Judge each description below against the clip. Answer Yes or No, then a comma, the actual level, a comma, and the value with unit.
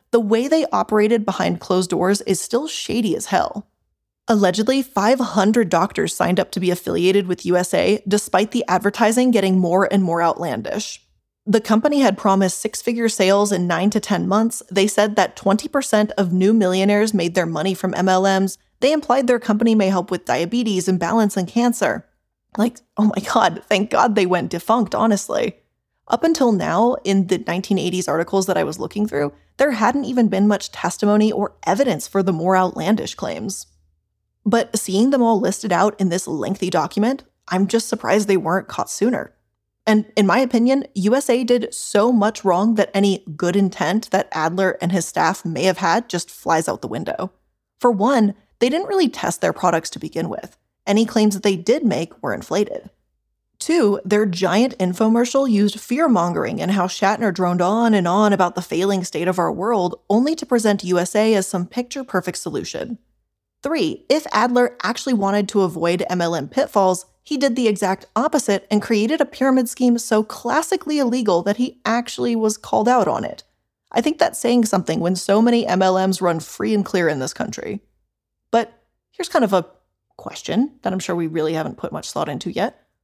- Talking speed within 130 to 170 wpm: No, average, 185 wpm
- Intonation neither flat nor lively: Yes, average, 4.0 semitones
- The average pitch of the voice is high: Yes, high, 205 Hz